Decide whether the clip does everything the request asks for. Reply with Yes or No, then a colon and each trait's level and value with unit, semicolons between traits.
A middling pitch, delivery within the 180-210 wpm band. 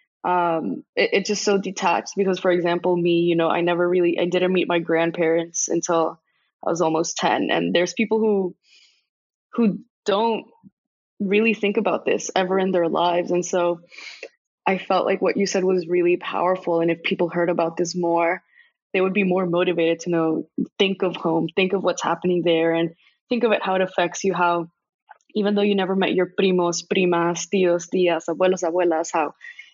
Yes: medium, 180 Hz; average, 190 wpm